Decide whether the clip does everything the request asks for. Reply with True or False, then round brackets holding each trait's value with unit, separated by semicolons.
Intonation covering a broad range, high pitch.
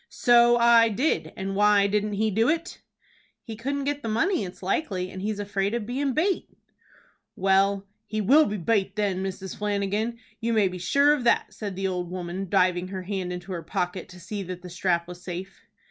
False (3.8 semitones; 200 Hz)